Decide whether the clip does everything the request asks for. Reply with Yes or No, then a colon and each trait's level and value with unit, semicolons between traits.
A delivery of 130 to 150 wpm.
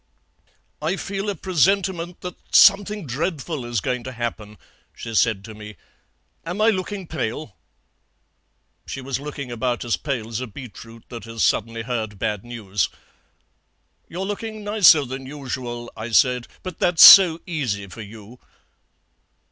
Yes: average, 145 wpm